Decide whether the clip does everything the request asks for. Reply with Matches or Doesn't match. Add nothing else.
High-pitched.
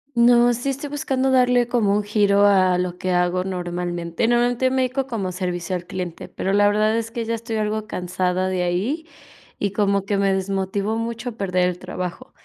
Matches